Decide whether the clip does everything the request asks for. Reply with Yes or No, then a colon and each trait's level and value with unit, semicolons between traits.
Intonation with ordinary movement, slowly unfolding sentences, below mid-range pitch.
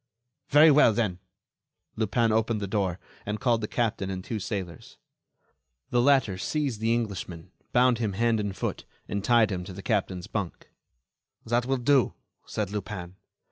No: average, 3.7 semitones; average, 160 wpm; low, 110 Hz